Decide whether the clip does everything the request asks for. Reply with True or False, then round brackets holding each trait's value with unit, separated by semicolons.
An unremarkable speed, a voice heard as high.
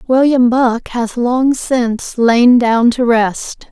True (145 wpm; 240 Hz)